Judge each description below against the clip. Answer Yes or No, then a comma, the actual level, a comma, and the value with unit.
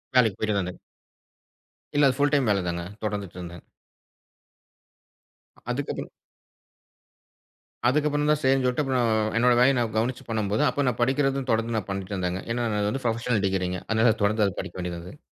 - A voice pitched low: Yes, low, 115 Hz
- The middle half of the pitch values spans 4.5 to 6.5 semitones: Yes, average, 5.1 semitones